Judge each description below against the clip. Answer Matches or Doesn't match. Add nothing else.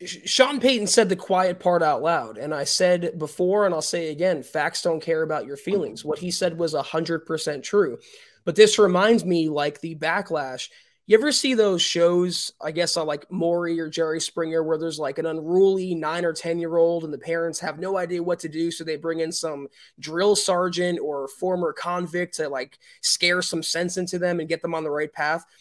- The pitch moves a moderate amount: Doesn't match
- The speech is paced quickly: Matches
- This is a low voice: Doesn't match